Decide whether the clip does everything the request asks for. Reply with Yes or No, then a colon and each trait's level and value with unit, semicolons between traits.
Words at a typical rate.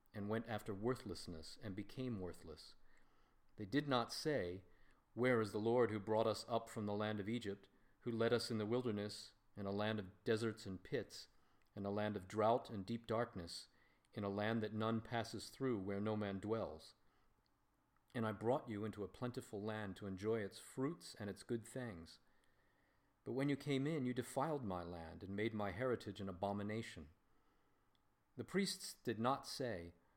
Yes: average, 185 wpm